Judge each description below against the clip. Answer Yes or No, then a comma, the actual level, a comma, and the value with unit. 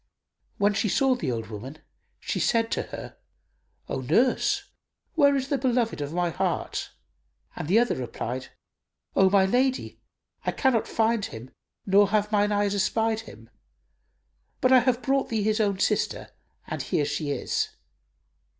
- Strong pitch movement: Yes, wide, 6.1 semitones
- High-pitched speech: Yes, high, 210 Hz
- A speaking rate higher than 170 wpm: No, average, 155 wpm